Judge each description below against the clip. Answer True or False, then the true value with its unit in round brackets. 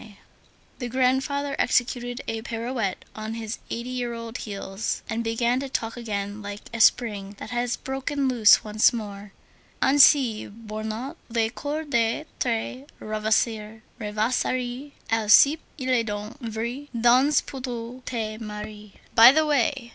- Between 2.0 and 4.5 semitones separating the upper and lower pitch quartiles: True (2.9 semitones)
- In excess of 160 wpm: False (140 wpm)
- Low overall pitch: False (235 Hz)